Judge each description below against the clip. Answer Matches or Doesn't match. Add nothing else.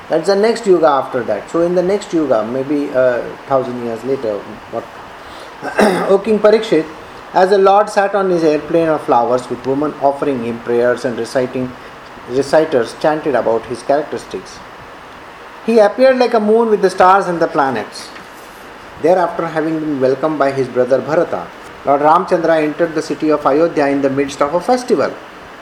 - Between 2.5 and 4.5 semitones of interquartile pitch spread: Doesn't match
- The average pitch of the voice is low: Doesn't match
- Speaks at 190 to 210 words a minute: Doesn't match